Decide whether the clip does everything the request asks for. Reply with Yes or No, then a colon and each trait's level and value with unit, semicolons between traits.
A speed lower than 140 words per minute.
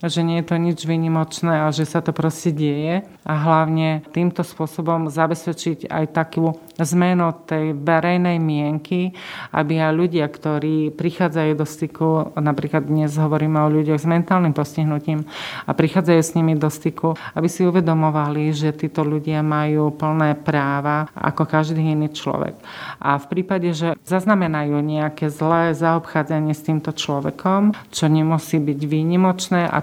No: average, 145 wpm